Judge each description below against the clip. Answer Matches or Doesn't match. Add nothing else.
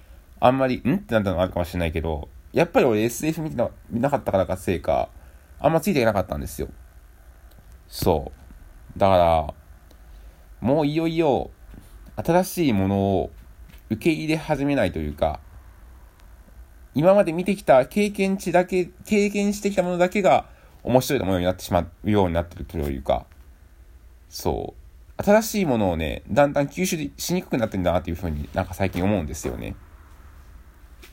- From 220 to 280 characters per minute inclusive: Doesn't match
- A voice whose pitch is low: Matches